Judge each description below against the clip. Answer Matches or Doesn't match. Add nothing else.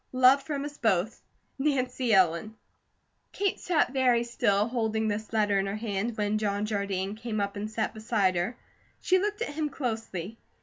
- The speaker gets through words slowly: Doesn't match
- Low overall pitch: Doesn't match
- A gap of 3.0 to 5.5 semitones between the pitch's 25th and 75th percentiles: Matches